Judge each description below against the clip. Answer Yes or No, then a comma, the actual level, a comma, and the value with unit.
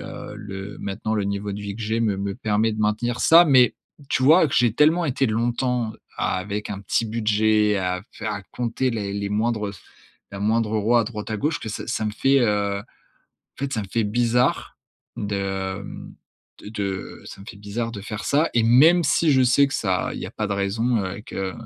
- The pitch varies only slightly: No, average, 3.0 semitones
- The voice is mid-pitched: No, low, 110 Hz